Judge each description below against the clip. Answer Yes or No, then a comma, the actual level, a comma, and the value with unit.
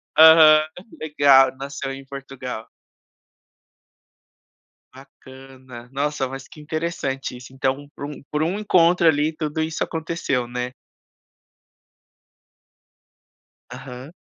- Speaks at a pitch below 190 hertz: Yes, medium, 140 Hz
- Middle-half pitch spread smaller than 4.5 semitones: Yes, average, 3.0 semitones